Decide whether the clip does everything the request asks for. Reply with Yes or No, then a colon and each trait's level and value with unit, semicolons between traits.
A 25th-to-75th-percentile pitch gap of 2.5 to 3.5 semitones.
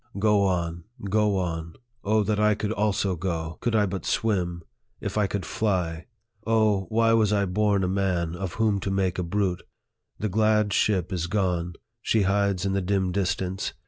Yes: average, 2.8 semitones